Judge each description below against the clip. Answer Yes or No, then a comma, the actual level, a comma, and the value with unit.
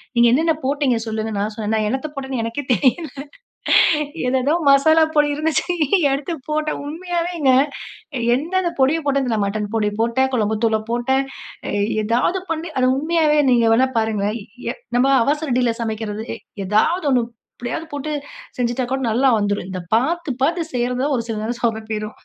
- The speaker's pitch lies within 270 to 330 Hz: No, very high, 255 Hz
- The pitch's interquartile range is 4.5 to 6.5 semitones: Yes, average, 5.1 semitones